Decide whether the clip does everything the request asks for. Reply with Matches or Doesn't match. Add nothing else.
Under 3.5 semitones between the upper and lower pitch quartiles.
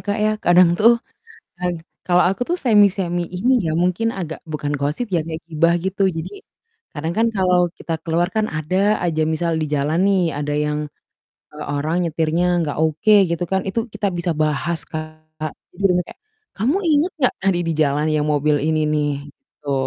Doesn't match